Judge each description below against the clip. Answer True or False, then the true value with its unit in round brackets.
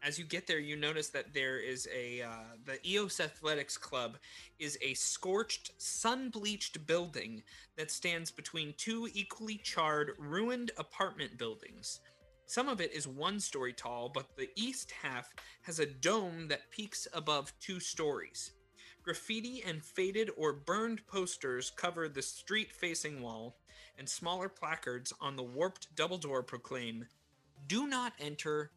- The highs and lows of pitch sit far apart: True (6.5 semitones)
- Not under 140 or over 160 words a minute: True (150 wpm)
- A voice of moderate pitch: True (160 Hz)